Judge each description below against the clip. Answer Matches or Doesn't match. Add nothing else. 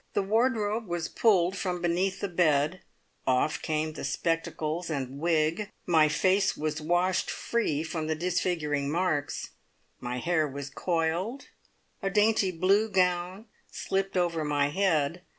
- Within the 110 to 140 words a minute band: Matches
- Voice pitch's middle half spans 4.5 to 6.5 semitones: Doesn't match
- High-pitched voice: Doesn't match